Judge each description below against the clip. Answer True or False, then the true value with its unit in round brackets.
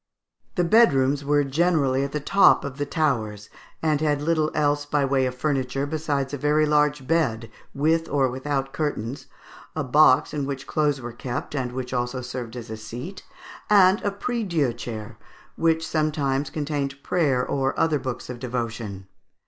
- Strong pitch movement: False (3.3 semitones)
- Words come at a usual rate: True (165 wpm)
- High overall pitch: False (140 Hz)